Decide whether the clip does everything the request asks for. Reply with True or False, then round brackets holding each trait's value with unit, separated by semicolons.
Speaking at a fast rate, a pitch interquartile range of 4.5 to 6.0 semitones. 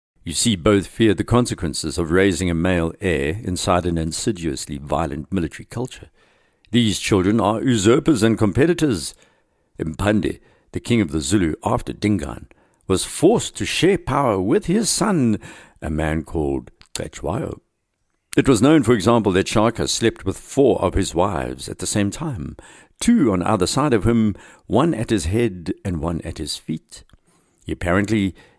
False (160 wpm; 5.3 semitones)